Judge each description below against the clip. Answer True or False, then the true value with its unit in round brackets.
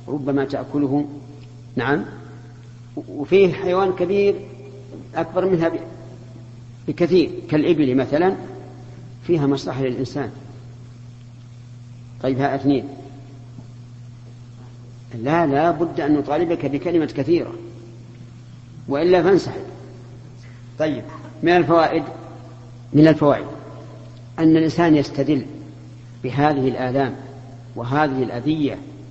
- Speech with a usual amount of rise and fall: True (3.7 semitones)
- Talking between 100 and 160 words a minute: False (80 wpm)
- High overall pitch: False (130 Hz)